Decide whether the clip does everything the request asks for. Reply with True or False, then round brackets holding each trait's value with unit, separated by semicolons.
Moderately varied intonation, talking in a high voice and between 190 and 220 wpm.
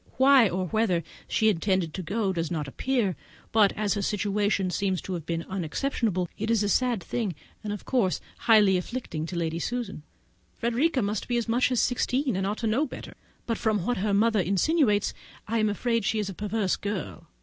True (3.7 semitones; 210 Hz; 200 wpm)